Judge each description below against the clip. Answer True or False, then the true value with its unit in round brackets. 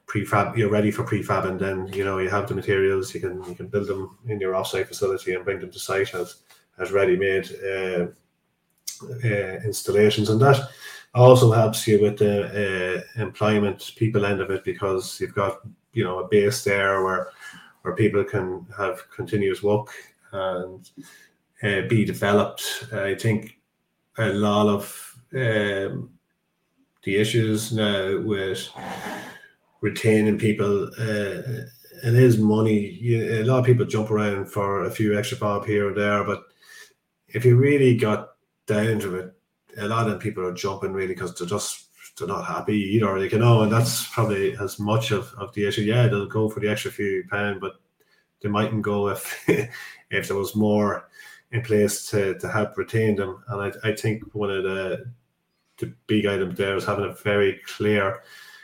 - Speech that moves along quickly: False (175 wpm)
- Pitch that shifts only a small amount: True (2.1 semitones)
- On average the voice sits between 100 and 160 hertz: True (105 Hz)